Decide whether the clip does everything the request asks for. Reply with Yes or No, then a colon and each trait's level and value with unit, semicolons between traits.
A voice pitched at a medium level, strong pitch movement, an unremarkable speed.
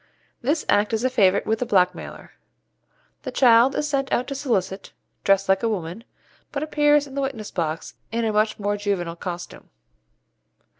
No: high, 220 Hz; wide, 5.7 semitones; average, 170 wpm